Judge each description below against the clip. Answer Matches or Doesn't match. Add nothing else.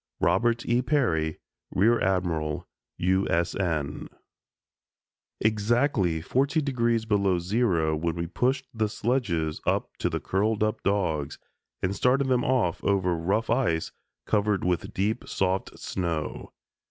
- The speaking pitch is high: Doesn't match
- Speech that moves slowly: Matches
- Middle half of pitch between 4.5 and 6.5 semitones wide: Matches